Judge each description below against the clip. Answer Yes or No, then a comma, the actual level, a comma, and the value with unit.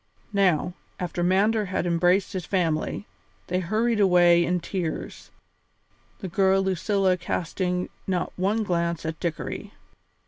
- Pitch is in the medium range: Yes, medium, 180 Hz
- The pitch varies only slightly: Yes, narrow, 2.0 semitones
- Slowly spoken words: Yes, slow, 125 wpm